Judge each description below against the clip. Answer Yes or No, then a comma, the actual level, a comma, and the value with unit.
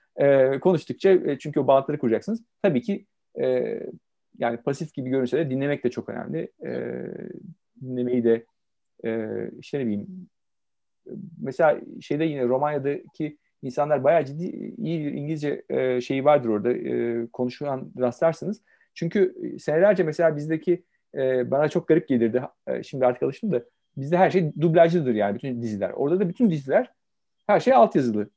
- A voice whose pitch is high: No, medium, 145 Hz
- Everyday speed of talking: No, fast, 145 wpm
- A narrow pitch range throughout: No, wide, 5.6 semitones